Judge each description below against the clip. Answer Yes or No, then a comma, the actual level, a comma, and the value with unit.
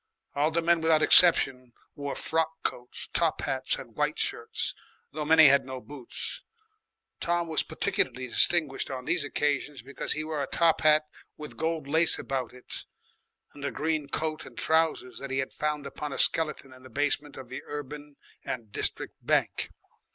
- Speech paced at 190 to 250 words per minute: No, average, 175 wpm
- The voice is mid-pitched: Yes, medium, 145 Hz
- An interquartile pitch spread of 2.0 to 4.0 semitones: Yes, average, 2.9 semitones